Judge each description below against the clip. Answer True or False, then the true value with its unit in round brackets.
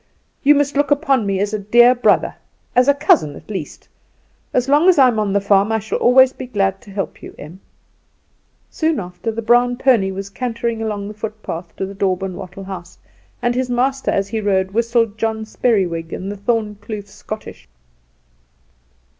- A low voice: False (215 Hz)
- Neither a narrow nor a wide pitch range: True (3.9 semitones)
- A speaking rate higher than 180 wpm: True (190 wpm)